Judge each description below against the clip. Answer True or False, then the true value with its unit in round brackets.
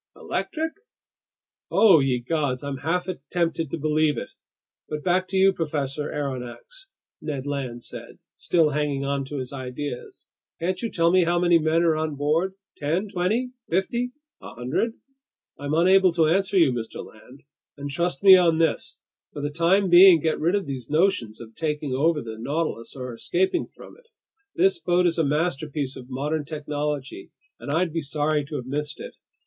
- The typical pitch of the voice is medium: True (155 Hz)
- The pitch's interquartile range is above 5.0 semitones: False (4.1 semitones)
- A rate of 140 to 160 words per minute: False (175 wpm)